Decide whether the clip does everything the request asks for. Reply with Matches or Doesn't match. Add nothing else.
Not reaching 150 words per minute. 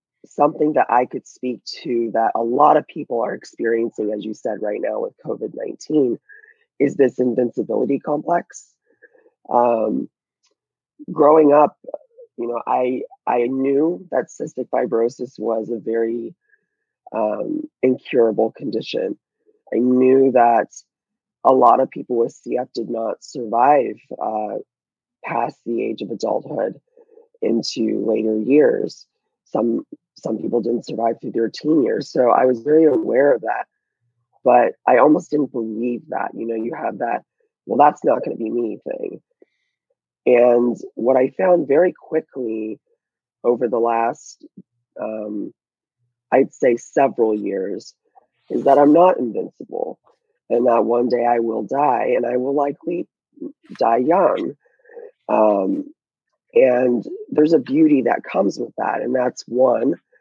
Matches